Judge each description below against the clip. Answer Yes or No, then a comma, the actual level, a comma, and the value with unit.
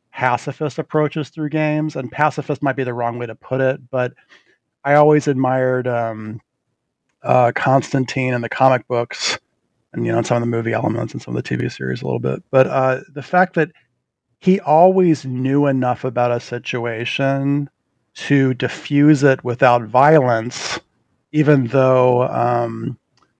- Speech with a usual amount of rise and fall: Yes, average, 3.1 semitones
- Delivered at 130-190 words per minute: Yes, average, 160 wpm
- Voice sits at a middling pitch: No, low, 130 Hz